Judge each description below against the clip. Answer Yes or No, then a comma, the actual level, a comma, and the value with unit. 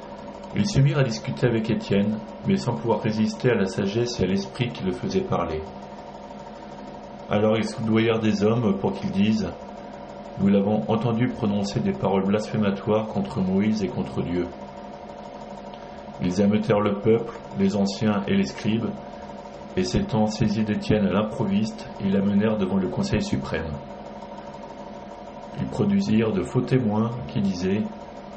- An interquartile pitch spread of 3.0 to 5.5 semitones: No, narrow, 2.5 semitones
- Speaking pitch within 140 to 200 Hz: No, low, 110 Hz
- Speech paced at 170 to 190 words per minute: No, slow, 145 wpm